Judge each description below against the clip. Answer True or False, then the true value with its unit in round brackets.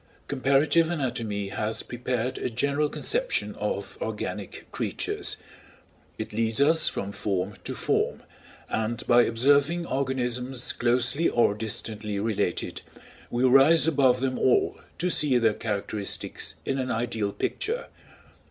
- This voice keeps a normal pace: False (125 wpm)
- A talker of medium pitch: False (125 Hz)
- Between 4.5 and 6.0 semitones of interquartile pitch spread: False (4.1 semitones)